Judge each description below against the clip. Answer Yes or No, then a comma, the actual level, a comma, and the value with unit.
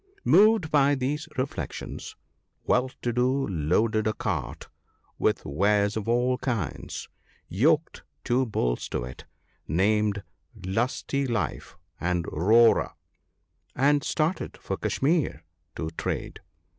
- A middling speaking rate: No, slow, 110 wpm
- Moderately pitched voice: No, low, 115 Hz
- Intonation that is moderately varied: No, wide, 5.9 semitones